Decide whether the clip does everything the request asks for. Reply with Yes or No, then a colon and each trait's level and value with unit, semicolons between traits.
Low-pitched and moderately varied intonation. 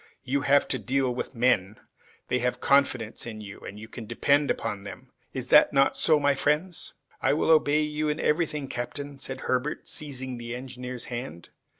Yes: low, 130 Hz; average, 3.0 semitones